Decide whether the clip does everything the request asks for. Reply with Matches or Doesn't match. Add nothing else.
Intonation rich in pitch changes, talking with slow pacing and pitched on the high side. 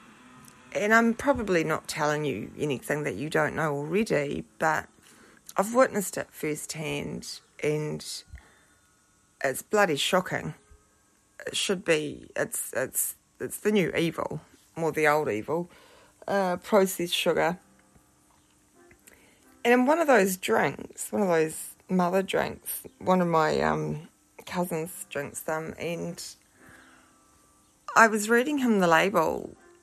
Doesn't match